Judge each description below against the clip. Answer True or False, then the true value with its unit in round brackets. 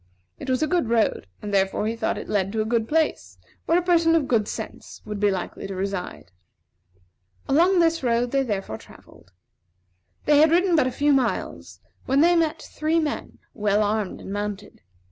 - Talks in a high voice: True (240 Hz)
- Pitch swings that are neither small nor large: False (7.3 semitones)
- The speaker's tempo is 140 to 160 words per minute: False (190 wpm)